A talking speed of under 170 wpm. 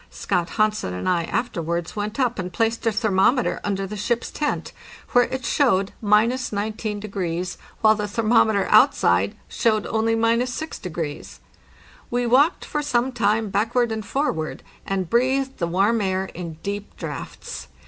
Yes: average, 150 wpm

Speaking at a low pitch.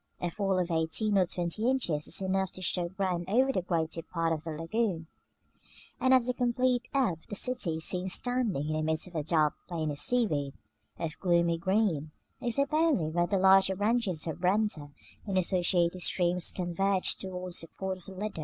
No: medium, 185 Hz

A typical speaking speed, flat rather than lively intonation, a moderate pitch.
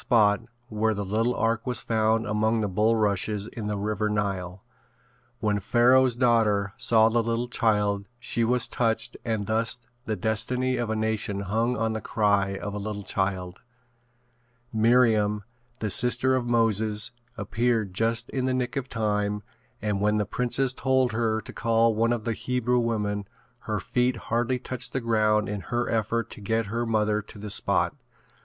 No: average, 170 wpm; narrow, 2.2 semitones; low, 110 Hz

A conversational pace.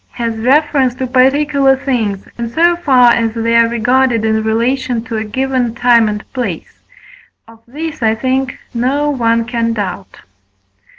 Yes: average, 155 wpm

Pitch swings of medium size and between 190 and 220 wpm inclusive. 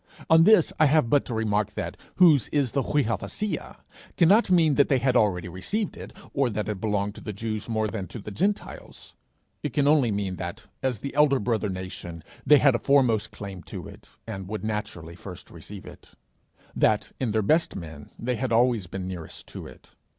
No: wide, 6.0 semitones; fast, 205 wpm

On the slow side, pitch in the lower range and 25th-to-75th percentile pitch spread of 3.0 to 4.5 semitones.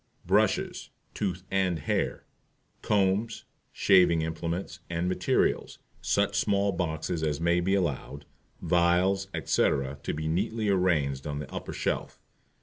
Yes: slow, 125 wpm; very low, 90 Hz; average, 3.4 semitones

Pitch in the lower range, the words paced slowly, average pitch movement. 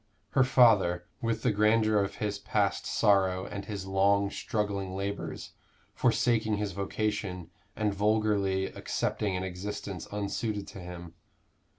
No: low, 100 Hz; slow, 125 wpm; narrow, 1.9 semitones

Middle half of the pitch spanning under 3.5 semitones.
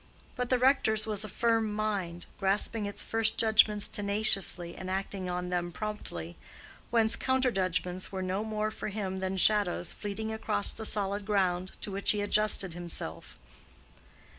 Yes: narrow, 2.6 semitones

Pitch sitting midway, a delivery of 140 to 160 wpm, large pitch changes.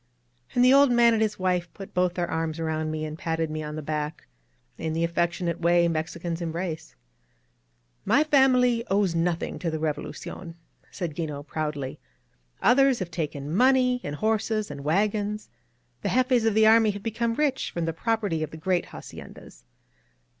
No: medium, 175 Hz; average, 175 wpm; wide, 5.9 semitones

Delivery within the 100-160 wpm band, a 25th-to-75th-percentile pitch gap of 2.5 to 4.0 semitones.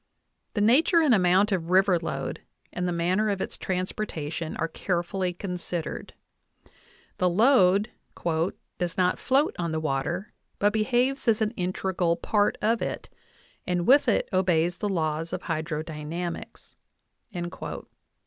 Yes: average, 140 wpm; average, 3.7 semitones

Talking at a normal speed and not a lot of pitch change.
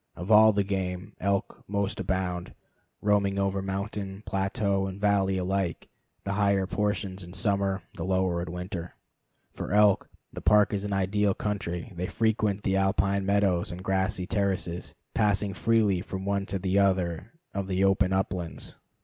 Yes: average, 160 wpm; narrow, 1.4 semitones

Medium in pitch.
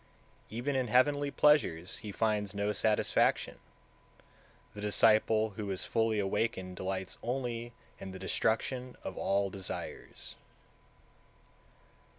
No: low, 110 Hz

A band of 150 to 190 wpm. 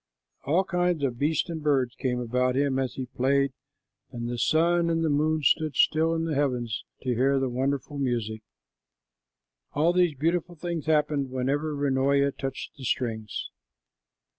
Yes: average, 160 wpm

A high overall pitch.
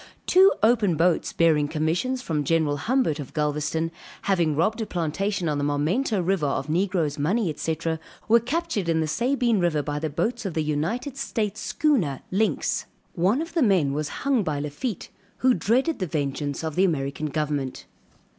No: medium, 170 Hz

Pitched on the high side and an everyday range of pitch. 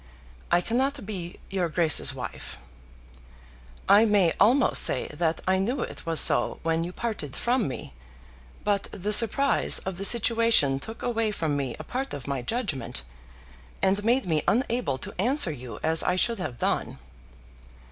No: high, 195 Hz; wide, 6.5 semitones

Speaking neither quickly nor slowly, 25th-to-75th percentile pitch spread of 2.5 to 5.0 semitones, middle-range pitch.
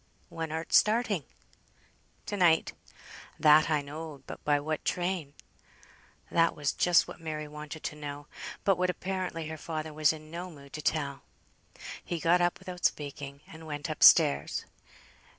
Yes: average, 155 wpm; average, 2.8 semitones; medium, 155 Hz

